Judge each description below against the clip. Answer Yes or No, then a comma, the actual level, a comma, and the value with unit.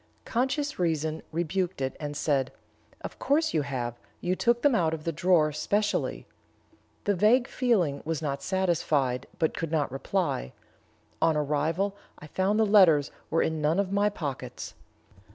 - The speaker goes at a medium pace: Yes, average, 155 wpm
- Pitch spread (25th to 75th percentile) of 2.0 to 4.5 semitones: No, average, 5.2 semitones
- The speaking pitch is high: No, medium, 165 Hz